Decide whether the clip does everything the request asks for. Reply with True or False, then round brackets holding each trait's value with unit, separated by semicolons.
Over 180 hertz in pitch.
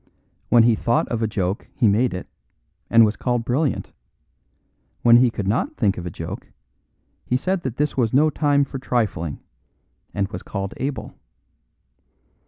False (115 Hz)